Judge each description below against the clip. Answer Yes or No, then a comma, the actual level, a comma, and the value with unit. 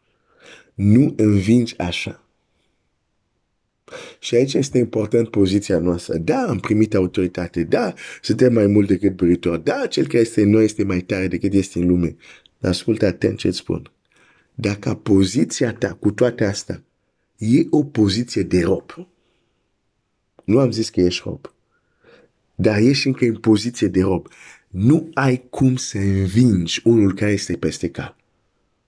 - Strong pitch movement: No, average, 4.0 semitones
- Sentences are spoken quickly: No, average, 145 wpm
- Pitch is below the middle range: Yes, low, 105 Hz